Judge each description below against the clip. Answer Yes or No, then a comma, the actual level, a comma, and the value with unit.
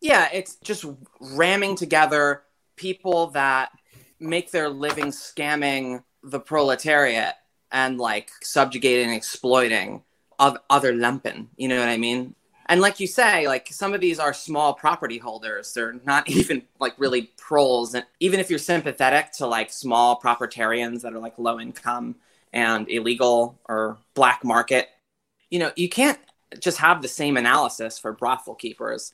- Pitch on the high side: No, low, 135 Hz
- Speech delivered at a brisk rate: No, average, 150 wpm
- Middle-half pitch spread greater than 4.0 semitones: Yes, average, 4.7 semitones